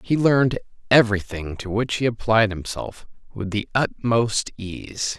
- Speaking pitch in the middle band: No, low, 110 Hz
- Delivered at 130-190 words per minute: Yes, average, 150 wpm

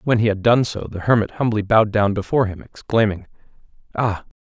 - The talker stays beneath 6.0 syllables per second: No, 6.1 syllables/s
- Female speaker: No, male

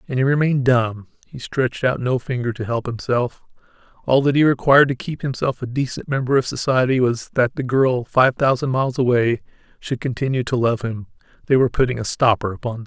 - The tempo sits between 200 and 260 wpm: Yes, fast, 205 wpm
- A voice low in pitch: Yes, low, 125 Hz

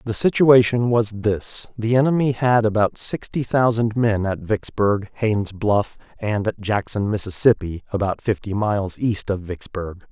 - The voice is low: Yes, low, 105 Hz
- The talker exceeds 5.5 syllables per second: No, 4.4 syllables/s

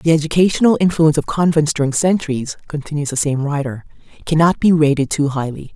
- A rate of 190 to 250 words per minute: No, average, 165 wpm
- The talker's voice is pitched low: No, medium, 155 Hz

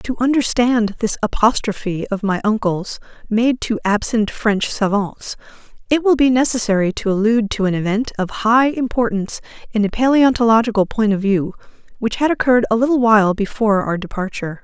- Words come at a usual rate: Yes, average, 160 wpm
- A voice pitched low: No, high, 220 Hz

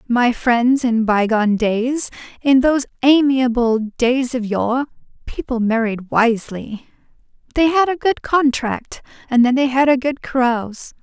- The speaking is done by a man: No, female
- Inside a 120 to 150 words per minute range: Yes, average, 140 wpm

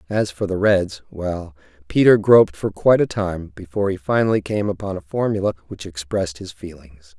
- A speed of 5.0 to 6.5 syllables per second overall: Yes, 5.5 syllables/s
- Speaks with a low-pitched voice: Yes, very low, 95 Hz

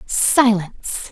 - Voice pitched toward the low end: No, high, 215 Hz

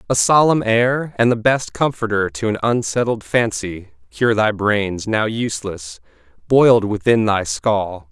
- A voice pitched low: Yes, low, 110 Hz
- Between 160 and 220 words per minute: No, average, 150 wpm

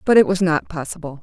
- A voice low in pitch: No, medium, 170 Hz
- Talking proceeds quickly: Yes, fast, 245 wpm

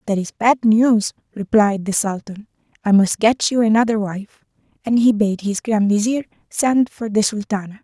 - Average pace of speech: Yes, average, 175 wpm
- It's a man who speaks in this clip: No, female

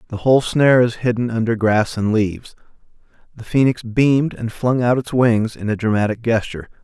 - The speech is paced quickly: No, average, 185 wpm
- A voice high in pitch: No, low, 115 Hz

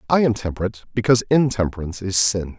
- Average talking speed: Yes, average, 160 wpm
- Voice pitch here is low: Yes, low, 105 Hz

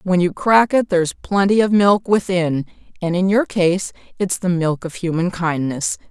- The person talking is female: Yes, female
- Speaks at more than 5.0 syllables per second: No, 4.6 syllables/s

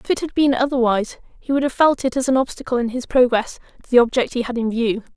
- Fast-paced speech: Yes, fast, 265 wpm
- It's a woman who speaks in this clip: Yes, female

